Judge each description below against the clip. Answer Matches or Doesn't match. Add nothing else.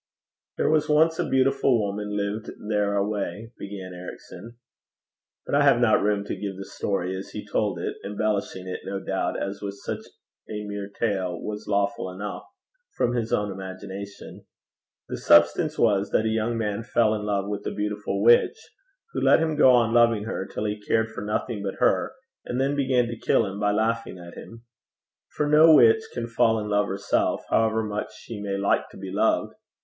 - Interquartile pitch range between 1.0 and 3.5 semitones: Matches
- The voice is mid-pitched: Doesn't match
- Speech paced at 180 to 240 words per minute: Matches